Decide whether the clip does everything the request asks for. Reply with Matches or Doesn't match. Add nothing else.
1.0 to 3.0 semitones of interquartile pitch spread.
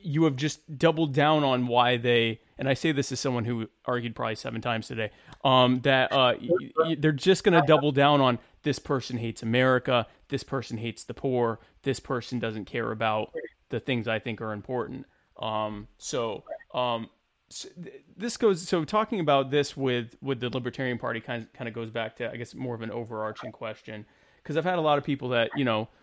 Doesn't match